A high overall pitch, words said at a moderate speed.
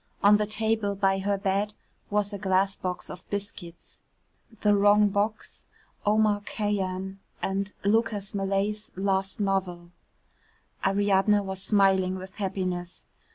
No: high, 200 Hz; slow, 120 wpm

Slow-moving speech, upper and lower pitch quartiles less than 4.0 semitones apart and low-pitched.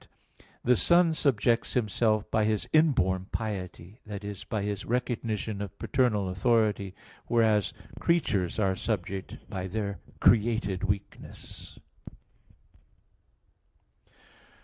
Yes: slow, 100 wpm; average, 3.1 semitones; low, 105 Hz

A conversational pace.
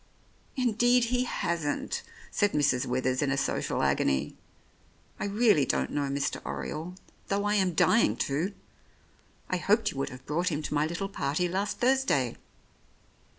Yes: average, 150 wpm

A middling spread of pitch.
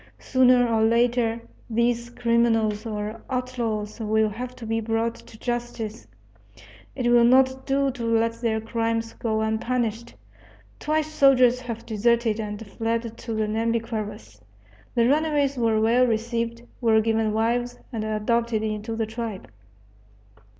No: narrow, 1.7 semitones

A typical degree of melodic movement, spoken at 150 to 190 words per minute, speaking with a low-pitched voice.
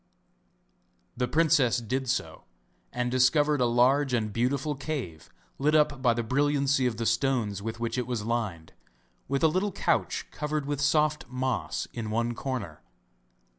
Yes: average, 3.7 semitones; average, 155 wpm; low, 130 Hz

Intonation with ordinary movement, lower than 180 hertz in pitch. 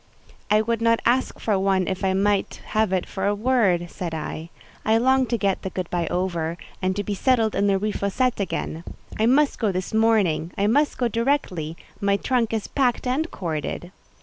No: average, 3.9 semitones; high, 205 Hz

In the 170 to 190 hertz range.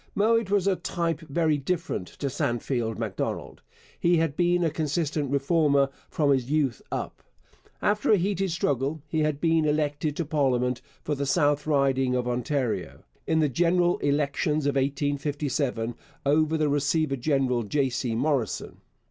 No: medium, 145 Hz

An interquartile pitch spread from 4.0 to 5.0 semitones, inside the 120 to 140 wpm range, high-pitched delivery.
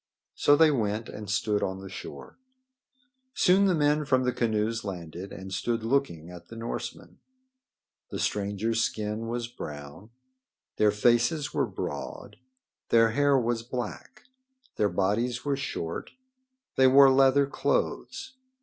No: average, 4.7 semitones; slow, 135 wpm; low, 115 Hz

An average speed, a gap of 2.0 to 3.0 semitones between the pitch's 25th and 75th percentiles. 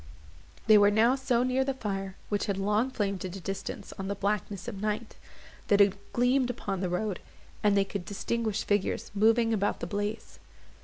Yes: average, 190 wpm; narrow, 2.5 semitones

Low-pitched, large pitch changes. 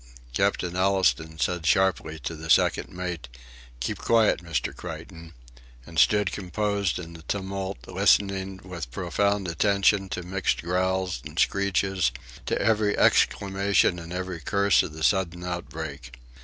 No: very low, 95 Hz; average, 2.9 semitones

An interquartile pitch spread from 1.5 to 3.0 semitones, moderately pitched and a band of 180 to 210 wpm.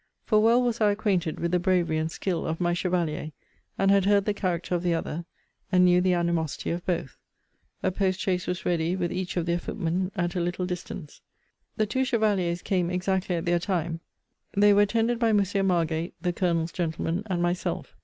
Yes: narrow, 2.4 semitones; medium, 180 Hz; average, 200 wpm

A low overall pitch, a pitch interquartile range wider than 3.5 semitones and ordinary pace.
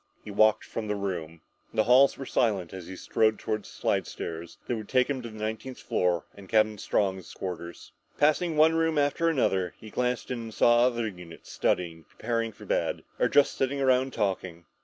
Yes: low, 110 Hz; average, 5.3 semitones; average, 195 wpm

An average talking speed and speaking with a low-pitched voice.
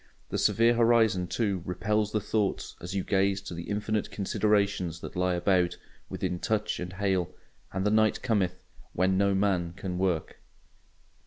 Yes: average, 160 wpm; very low, 95 Hz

